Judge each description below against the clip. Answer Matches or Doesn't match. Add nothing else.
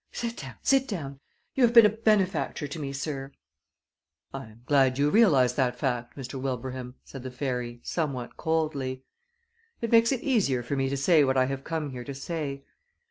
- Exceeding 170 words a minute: Matches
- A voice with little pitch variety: Doesn't match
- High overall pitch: Doesn't match